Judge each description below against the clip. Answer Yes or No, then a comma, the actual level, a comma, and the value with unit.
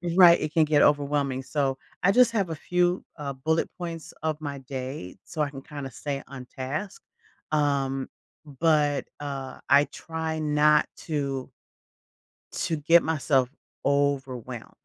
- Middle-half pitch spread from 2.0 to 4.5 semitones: Yes, average, 2.7 semitones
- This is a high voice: No, medium, 145 Hz